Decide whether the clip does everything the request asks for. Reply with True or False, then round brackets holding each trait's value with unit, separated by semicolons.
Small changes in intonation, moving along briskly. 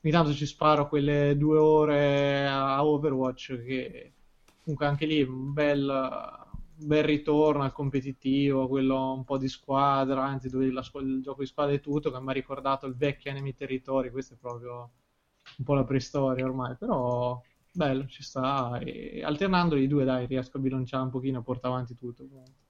True (1.9 semitones; 180 wpm)